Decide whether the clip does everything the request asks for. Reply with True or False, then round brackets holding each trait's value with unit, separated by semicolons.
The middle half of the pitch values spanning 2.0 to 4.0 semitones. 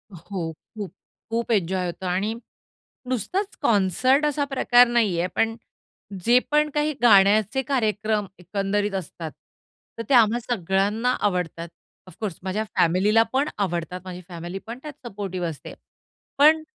False (4.8 semitones)